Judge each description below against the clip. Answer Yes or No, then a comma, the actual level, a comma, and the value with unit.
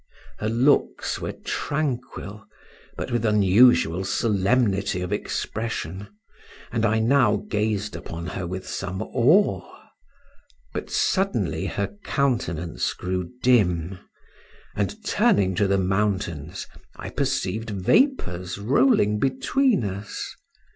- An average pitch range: Yes, average, 4.6 semitones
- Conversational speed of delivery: No, slow, 105 wpm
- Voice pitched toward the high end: No, low, 105 Hz